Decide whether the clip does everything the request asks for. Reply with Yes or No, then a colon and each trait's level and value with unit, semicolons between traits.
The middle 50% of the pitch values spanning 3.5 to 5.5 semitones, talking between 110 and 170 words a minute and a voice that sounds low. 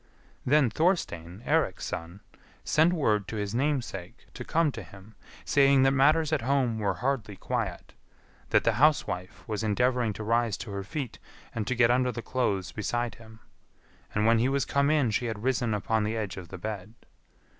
No: average, 4.3 semitones; average, 185 wpm; low, 115 Hz